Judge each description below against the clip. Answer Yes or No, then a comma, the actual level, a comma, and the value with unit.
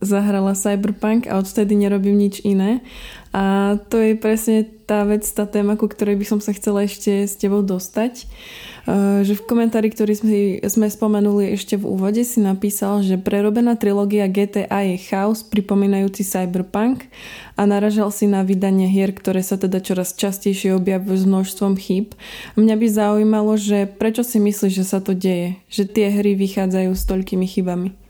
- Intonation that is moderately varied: No, narrow, 1.5 semitones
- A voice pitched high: Yes, high, 205 Hz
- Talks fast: Yes, fast, 170 wpm